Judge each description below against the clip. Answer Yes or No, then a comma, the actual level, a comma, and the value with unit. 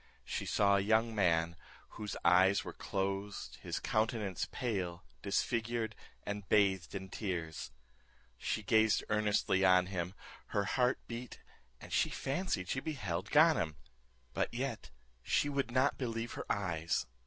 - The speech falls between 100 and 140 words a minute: Yes, slow, 135 wpm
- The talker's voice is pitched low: Yes, low, 105 Hz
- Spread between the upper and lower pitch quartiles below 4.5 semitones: Yes, average, 4.0 semitones